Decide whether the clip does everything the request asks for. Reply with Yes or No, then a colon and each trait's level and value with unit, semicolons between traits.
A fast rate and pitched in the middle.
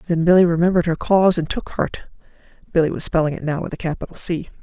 Yes: fast, 210 wpm; medium, 170 Hz